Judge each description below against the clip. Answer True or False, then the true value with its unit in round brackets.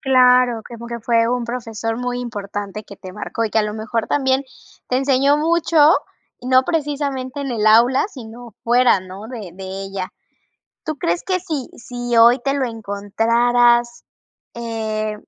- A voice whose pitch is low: False (240 Hz)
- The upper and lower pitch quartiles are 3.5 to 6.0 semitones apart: False (2.9 semitones)